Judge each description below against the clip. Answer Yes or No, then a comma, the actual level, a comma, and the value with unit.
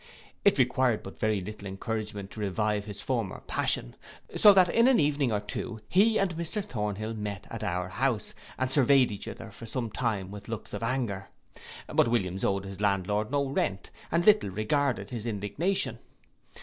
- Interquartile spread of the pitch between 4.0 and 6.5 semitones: Yes, average, 5.1 semitones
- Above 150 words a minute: Yes, average, 175 wpm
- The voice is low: Yes, low, 110 Hz